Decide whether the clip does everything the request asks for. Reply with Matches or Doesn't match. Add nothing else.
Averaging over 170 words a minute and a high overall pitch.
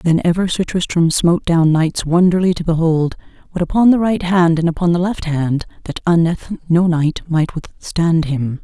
Doesn't match